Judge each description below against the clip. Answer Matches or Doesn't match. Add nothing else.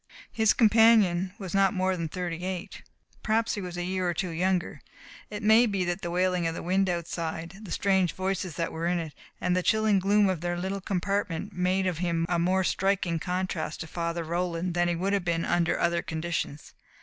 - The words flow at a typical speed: Doesn't match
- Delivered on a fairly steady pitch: Matches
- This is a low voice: Doesn't match